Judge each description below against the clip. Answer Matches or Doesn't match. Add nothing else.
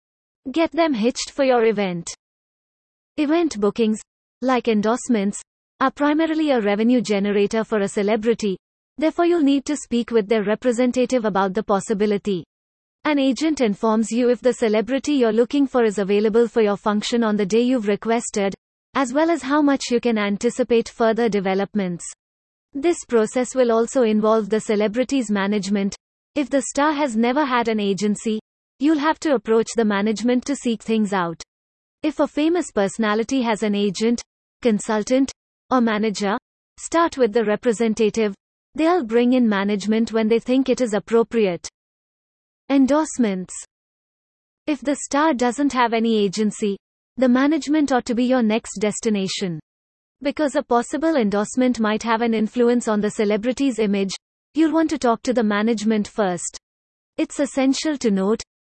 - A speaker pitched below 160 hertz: Doesn't match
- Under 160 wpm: Matches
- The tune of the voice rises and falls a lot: Doesn't match